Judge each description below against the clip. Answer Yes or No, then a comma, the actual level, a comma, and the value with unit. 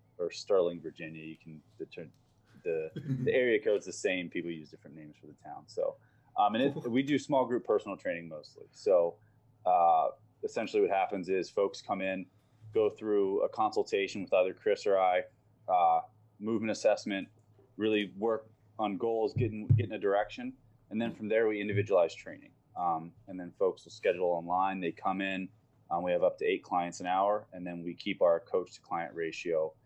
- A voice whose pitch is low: Yes, low, 120 Hz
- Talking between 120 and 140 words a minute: No, average, 190 wpm